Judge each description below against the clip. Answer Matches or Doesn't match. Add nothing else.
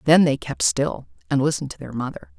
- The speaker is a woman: Matches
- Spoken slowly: Doesn't match